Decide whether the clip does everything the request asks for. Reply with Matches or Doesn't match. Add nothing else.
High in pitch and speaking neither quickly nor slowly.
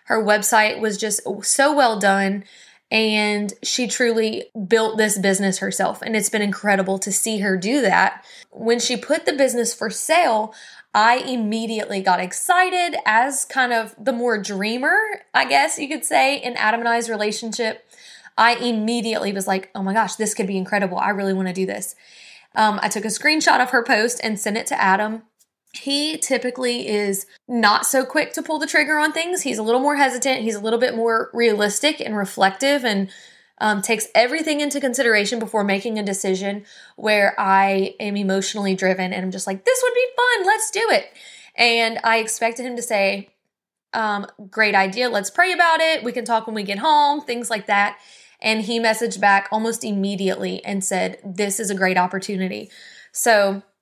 Matches